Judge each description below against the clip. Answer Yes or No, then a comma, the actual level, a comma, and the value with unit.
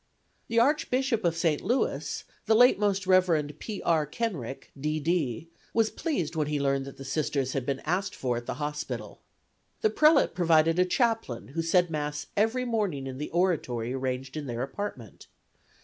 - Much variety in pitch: Yes, wide, 7.0 semitones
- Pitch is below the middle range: No, medium, 160 Hz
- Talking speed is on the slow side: No, average, 175 wpm